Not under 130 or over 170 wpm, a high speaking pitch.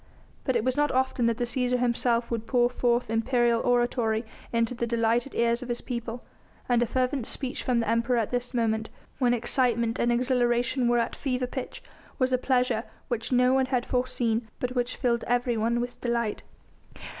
No: average, 185 wpm; high, 240 Hz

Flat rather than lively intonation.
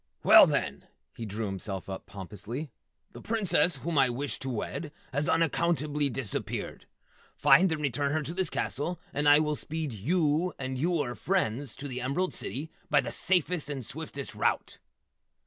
No: average, 4.3 semitones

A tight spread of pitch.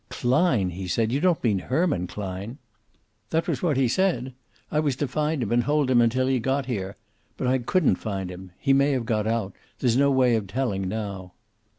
No: average, 5.2 semitones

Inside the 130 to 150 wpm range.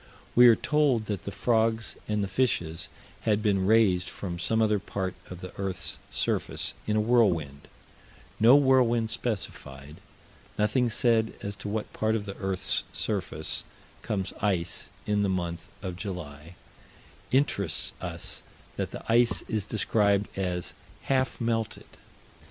Yes: average, 140 wpm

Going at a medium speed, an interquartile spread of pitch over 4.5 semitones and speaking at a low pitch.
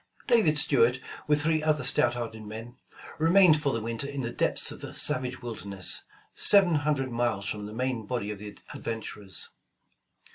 Yes: average, 175 wpm; average, 5.1 semitones; low, 125 Hz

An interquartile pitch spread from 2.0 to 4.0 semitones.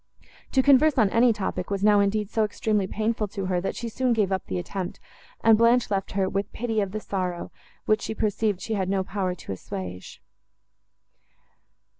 Yes: average, 2.8 semitones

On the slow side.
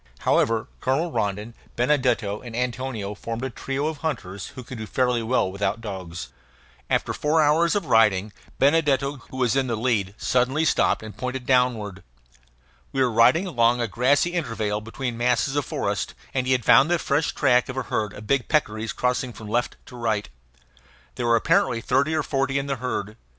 No: average, 185 wpm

